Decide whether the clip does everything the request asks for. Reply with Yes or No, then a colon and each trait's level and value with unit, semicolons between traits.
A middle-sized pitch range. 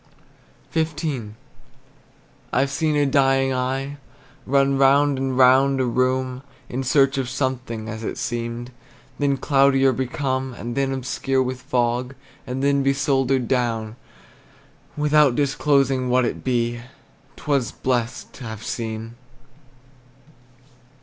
No: narrow, 1.9 semitones